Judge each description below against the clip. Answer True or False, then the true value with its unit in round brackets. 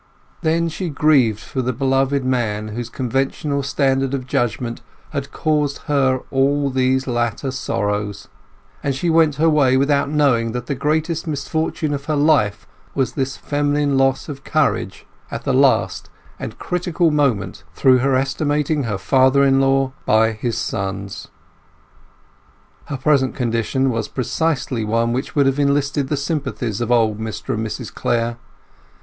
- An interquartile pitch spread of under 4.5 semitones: True (3.5 semitones)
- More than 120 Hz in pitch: True (135 Hz)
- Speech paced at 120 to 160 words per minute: True (150 wpm)